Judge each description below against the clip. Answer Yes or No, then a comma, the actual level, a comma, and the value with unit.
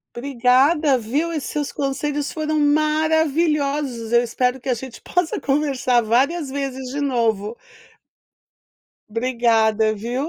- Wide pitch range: No, average, 3.8 semitones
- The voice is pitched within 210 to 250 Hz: No, very high, 270 Hz